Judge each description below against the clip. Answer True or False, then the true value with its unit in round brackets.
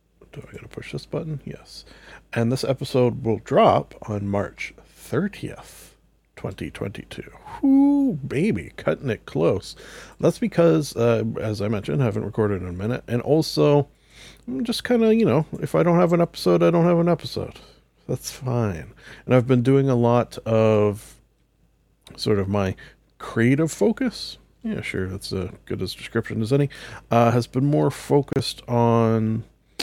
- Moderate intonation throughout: False (5.8 semitones)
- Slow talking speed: False (165 wpm)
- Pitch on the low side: True (125 Hz)